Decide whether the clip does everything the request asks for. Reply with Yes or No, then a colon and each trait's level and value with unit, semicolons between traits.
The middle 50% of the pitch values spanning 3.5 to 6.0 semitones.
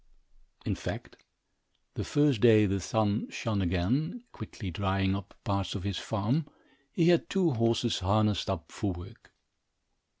Yes: average, 3.9 semitones